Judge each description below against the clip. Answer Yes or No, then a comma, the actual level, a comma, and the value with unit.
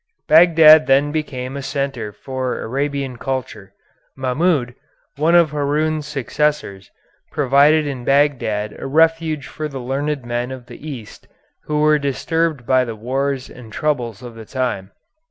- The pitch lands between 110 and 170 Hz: Yes, medium, 140 Hz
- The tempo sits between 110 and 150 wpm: Yes, average, 140 wpm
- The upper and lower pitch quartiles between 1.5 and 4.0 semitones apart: Yes, average, 3.4 semitones